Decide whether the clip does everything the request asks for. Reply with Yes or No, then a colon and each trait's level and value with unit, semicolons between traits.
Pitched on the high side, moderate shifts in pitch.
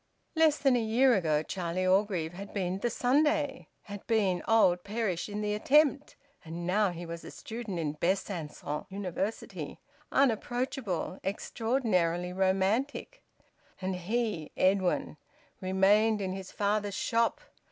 Yes: high, 200 Hz; average, 4.1 semitones